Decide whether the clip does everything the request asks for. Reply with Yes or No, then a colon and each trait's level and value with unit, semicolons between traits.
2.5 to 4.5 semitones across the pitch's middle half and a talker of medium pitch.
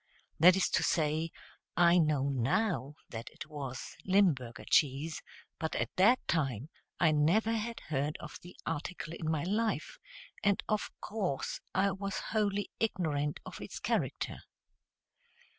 No: average, 5.2 semitones; medium, 165 Hz